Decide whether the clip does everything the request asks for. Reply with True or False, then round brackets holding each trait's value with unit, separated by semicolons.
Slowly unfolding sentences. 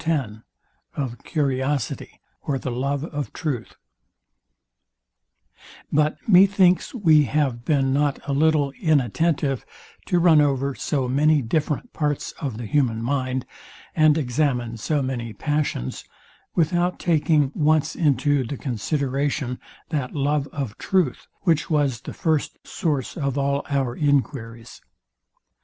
True (125 wpm)